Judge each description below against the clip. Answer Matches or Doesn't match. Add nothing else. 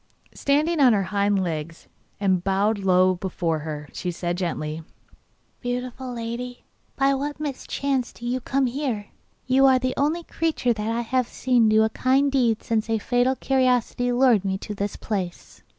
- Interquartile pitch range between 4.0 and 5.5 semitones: Matches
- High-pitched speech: Matches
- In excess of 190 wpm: Doesn't match